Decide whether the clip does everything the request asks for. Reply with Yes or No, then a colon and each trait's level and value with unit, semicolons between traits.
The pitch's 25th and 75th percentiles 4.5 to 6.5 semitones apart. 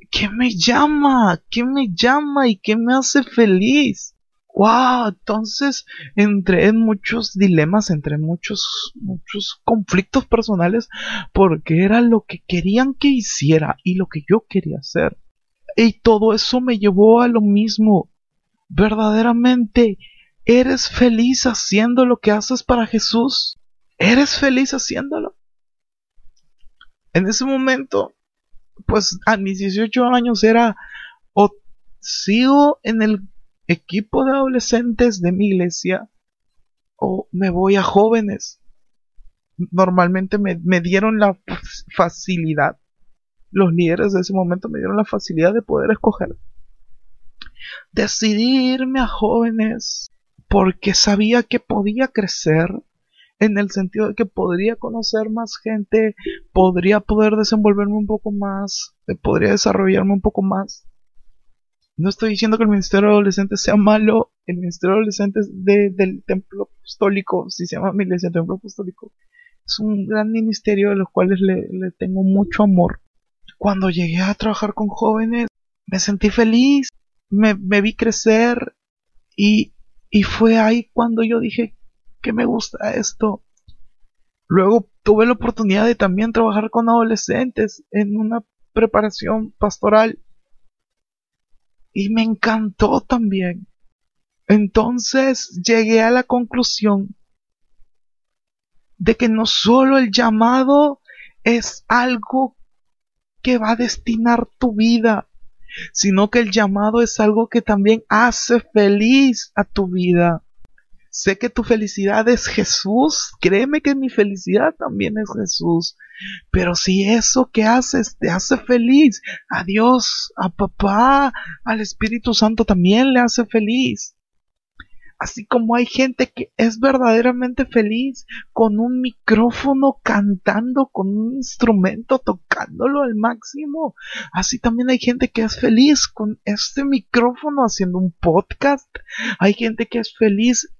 No: average, 3.3 semitones